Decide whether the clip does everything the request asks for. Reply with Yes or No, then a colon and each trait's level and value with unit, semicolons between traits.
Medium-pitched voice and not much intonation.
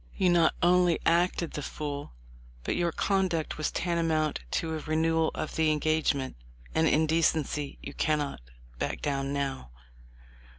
Yes: medium, 155 Hz; narrow, 2.1 semitones